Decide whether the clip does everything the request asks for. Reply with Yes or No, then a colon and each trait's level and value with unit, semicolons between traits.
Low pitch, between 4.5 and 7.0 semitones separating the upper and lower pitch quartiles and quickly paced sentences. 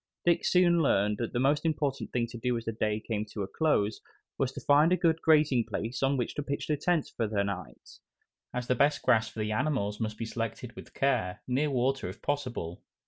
Yes: low, 125 Hz; average, 4.9 semitones; fast, 220 wpm